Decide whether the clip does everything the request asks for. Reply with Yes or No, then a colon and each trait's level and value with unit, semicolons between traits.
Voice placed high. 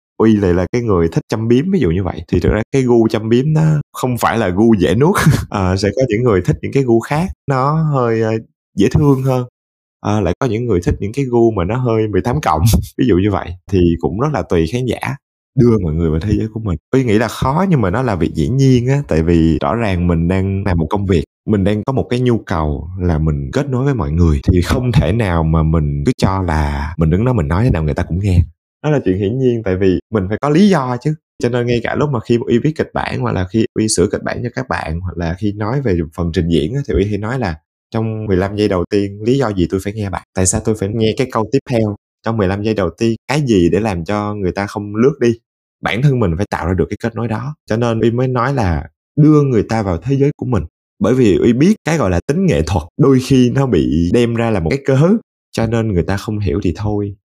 No: low, 110 Hz